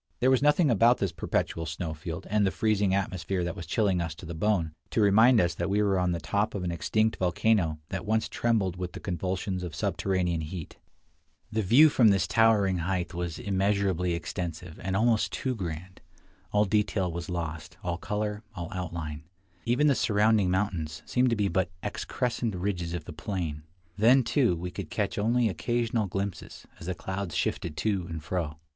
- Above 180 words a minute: Yes, average, 190 wpm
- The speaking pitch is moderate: No, very low, 95 Hz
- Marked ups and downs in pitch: No, average, 3.7 semitones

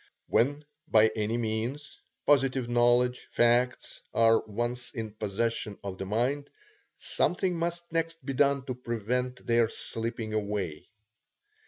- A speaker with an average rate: No, slow, 125 wpm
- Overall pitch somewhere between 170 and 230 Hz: No, low, 120 Hz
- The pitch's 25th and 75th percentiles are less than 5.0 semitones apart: Yes, average, 3.5 semitones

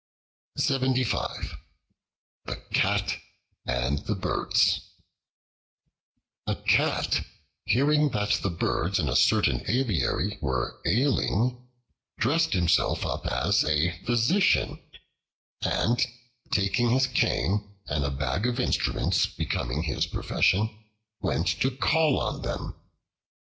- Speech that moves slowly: Yes, slow, 100 wpm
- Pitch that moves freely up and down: Yes, wide, 7.1 semitones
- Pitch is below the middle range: Yes, low, 105 Hz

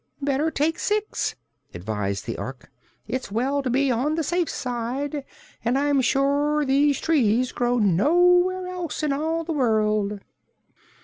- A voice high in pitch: Yes, very high, 275 Hz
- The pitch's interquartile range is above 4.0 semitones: Yes, average, 4.8 semitones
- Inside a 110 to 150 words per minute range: Yes, average, 140 wpm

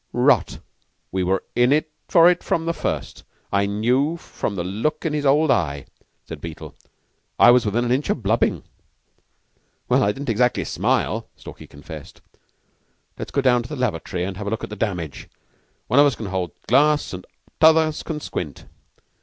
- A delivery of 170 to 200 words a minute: Yes, average, 180 wpm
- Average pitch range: No, wide, 7.3 semitones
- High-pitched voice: No, low, 120 Hz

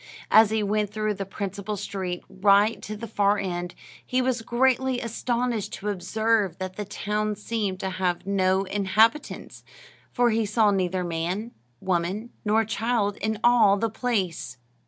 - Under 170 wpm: Yes, average, 155 wpm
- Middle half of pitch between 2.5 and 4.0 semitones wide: Yes, average, 2.9 semitones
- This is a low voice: No, high, 210 Hz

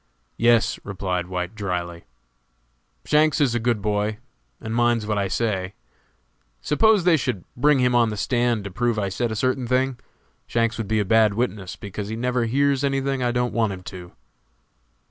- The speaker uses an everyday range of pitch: Yes, average, 3.8 semitones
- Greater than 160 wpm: Yes, average, 185 wpm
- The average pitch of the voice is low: Yes, low, 115 Hz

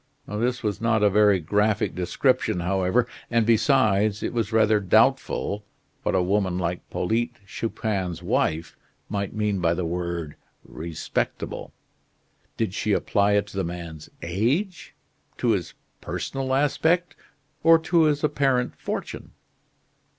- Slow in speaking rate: Yes, slow, 130 wpm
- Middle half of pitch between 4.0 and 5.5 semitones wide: Yes, average, 5.0 semitones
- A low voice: Yes, low, 105 Hz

